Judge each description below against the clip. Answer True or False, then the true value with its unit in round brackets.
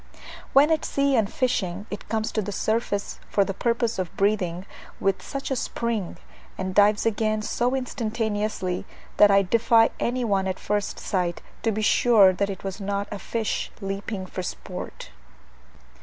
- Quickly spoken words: False (165 wpm)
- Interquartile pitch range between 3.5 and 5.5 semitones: False (2.8 semitones)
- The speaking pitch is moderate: False (210 Hz)